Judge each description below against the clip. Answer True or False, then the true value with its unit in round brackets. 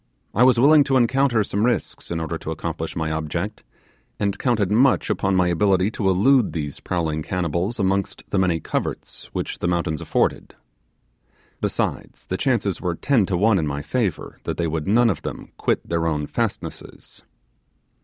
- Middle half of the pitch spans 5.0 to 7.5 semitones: True (5.4 semitones)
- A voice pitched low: True (95 Hz)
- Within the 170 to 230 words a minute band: True (175 wpm)